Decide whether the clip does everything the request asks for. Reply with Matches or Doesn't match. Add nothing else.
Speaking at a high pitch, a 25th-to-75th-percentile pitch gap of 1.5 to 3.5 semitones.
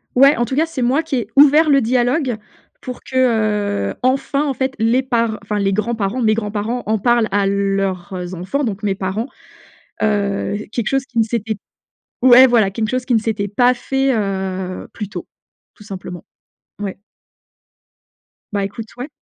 Doesn't match